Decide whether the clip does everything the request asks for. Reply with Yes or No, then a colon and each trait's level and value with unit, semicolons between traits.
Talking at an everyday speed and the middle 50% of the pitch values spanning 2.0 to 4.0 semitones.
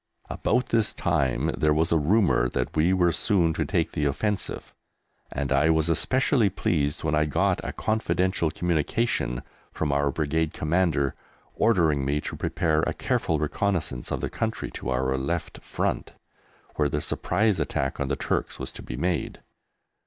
No: average, 165 wpm; average, 4.5 semitones